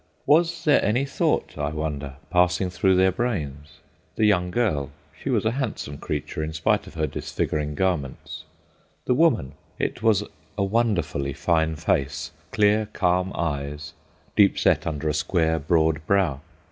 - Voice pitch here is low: Yes, very low, 85 Hz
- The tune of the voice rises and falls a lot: Yes, wide, 5.7 semitones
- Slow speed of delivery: No, average, 145 wpm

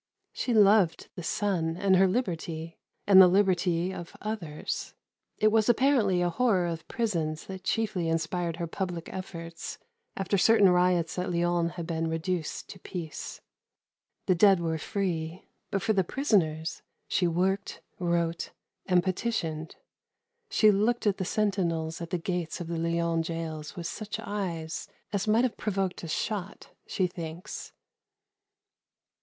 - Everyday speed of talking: Yes, average, 145 wpm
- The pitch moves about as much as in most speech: Yes, average, 3.2 semitones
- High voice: No, medium, 180 Hz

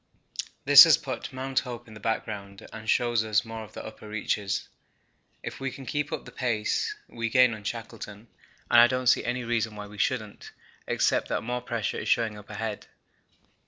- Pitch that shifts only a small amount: Yes, narrow, 2.3 semitones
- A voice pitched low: Yes, low, 115 Hz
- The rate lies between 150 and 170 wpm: No, average, 195 wpm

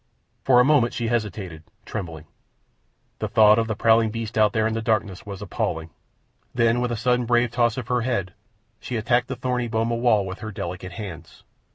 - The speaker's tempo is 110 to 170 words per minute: No, average, 195 wpm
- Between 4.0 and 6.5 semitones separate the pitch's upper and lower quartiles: No, average, 2.9 semitones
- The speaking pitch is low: Yes, low, 110 Hz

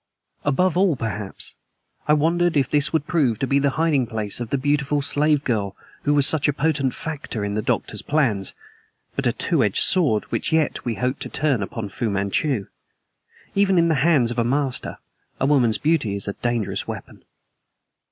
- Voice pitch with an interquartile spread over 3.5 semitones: Yes, average, 5.0 semitones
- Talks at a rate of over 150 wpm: Yes, average, 190 wpm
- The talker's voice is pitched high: No, medium, 140 Hz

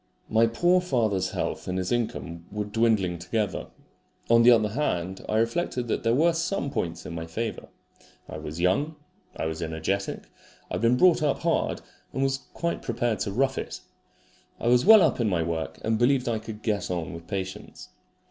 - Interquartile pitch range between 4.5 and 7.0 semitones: Yes, wide, 5.5 semitones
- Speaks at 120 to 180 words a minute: No, average, 190 wpm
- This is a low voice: Yes, low, 110 Hz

